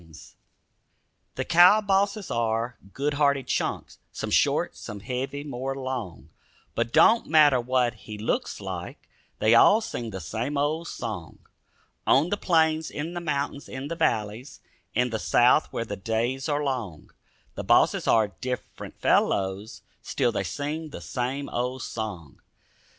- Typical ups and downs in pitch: Yes, average, 4.8 semitones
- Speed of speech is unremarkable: Yes, average, 150 wpm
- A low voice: Yes, low, 130 Hz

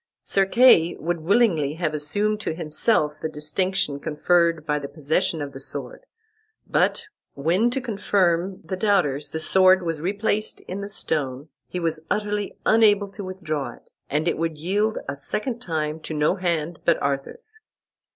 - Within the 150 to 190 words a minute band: Yes, average, 160 wpm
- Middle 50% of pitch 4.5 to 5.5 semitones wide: Yes, average, 4.8 semitones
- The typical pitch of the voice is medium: Yes, medium, 170 Hz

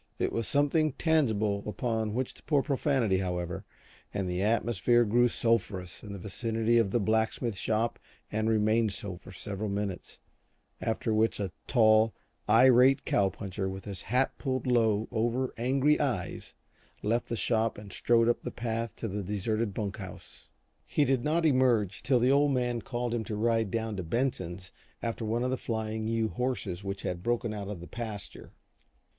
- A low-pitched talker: Yes, low, 110 Hz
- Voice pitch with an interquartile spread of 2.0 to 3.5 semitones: Yes, average, 3.2 semitones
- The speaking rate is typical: Yes, average, 175 wpm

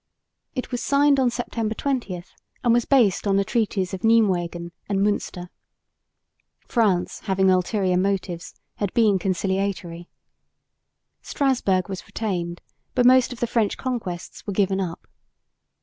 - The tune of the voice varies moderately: Yes, average, 4.3 semitones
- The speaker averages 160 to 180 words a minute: No, slow, 135 wpm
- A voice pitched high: Yes, high, 200 Hz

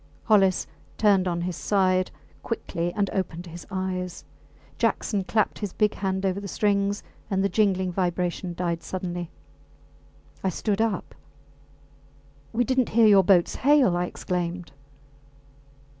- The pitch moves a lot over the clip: No, narrow, 2.5 semitones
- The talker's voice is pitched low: No, high, 190 Hz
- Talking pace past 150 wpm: No, slow, 135 wpm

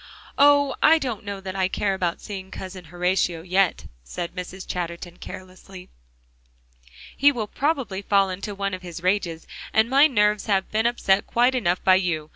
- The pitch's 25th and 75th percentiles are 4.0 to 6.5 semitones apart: No, average, 3.1 semitones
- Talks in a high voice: Yes, high, 195 Hz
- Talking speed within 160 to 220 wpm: Yes, average, 170 wpm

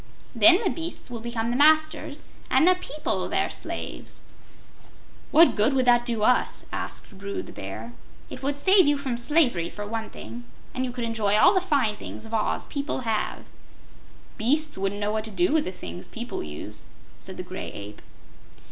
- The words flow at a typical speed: Yes, average, 185 wpm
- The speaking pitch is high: Yes, high, 240 Hz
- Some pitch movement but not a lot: No, wide, 6.2 semitones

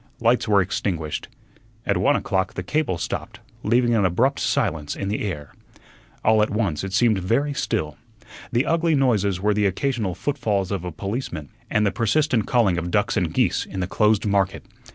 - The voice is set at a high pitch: No, low, 105 Hz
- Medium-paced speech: Yes, average, 180 wpm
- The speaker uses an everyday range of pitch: Yes, average, 4.1 semitones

